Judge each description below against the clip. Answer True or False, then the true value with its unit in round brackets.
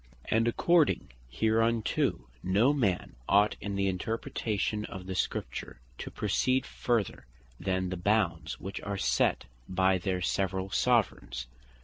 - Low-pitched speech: True (100 Hz)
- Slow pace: True (125 wpm)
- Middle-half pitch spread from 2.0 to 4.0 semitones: True (3.3 semitones)